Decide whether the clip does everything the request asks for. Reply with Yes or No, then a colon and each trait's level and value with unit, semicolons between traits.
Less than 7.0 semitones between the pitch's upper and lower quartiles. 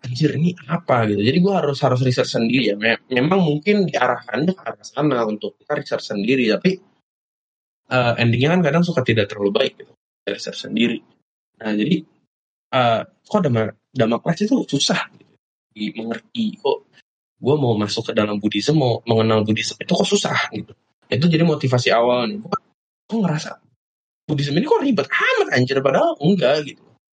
No: wide, 8.2 semitones